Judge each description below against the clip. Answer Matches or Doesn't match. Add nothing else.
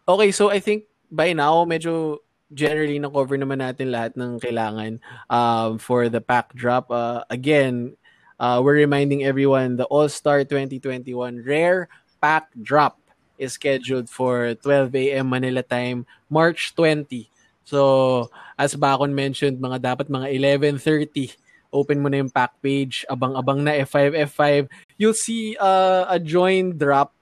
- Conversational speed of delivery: Matches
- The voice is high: Doesn't match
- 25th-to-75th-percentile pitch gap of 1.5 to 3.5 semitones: Matches